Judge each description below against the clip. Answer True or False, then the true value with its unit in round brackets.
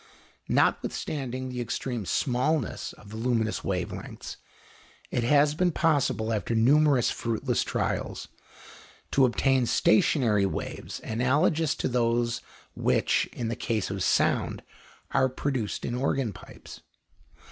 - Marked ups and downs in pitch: False (3.5 semitones)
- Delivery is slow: True (120 wpm)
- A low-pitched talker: True (125 Hz)